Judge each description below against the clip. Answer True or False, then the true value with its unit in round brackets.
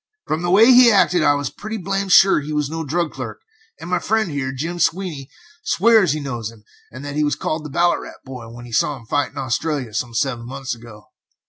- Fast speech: True (230 wpm)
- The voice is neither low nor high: True (150 Hz)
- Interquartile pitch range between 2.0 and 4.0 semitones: False (5.3 semitones)